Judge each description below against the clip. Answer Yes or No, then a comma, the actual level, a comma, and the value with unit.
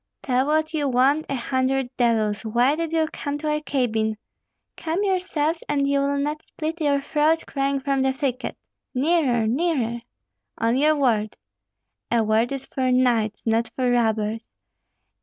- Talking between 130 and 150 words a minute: No, average, 160 wpm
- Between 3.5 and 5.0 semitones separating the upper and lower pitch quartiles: Yes, average, 4.1 semitones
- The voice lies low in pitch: No, very high, 270 Hz